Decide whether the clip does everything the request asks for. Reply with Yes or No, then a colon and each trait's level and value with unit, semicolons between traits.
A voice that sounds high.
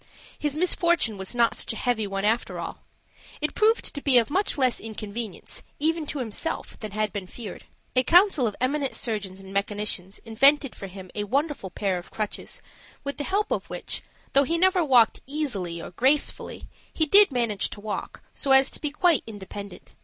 Yes: high, 240 Hz